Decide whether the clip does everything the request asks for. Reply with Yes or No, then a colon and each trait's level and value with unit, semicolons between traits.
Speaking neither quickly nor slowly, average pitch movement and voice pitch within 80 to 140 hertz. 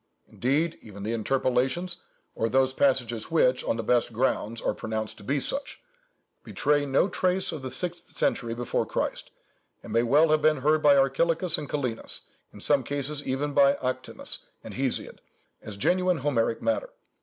Yes: average, 160 wpm; average, 4.3 semitones; low, 135 Hz